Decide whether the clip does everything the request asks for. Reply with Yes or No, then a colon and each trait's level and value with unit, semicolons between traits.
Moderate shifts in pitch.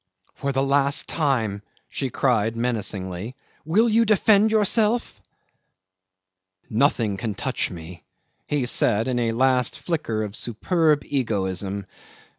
No: wide, 5.9 semitones